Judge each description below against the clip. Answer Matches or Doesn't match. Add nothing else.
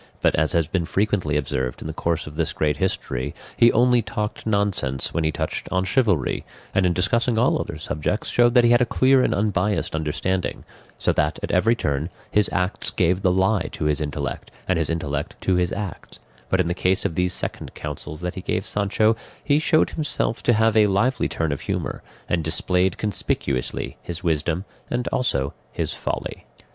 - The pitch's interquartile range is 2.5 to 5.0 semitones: Doesn't match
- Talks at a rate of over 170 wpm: Matches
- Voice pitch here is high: Doesn't match